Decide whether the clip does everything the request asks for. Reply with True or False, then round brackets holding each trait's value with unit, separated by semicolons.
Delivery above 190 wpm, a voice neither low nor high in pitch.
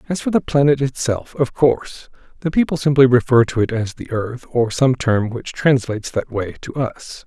False (200 wpm; 130 Hz)